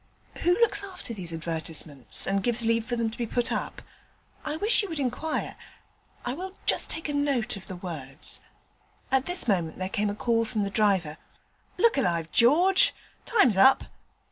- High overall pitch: Yes, high, 230 Hz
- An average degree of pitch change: No, wide, 8.2 semitones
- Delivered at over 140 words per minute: Yes, average, 180 wpm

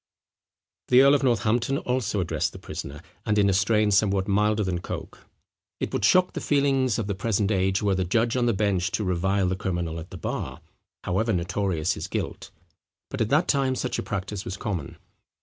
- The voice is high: No, low, 100 Hz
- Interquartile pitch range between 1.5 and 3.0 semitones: No, average, 3.9 semitones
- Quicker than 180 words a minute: Yes, average, 200 wpm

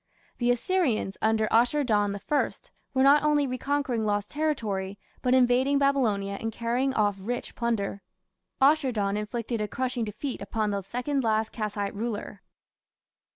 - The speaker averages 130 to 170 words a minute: Yes, average, 145 wpm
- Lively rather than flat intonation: No, average, 4.2 semitones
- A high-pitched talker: Yes, high, 235 Hz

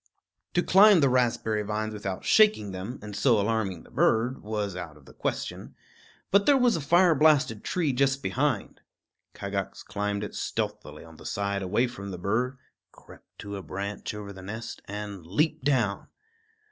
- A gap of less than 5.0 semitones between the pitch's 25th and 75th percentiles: No, average, 5.3 semitones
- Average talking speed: Yes, average, 170 wpm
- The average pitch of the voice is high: No, low, 110 Hz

